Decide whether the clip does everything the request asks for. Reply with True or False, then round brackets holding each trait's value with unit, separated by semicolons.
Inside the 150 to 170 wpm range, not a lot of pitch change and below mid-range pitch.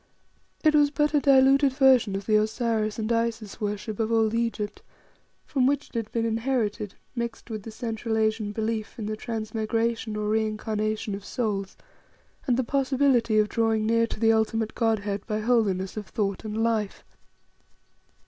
False (165 wpm; 1.6 semitones; 225 Hz)